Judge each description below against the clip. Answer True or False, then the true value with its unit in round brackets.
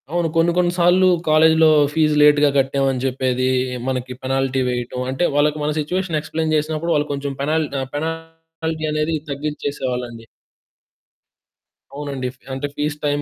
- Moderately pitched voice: True (150 Hz)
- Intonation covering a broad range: False (3.2 semitones)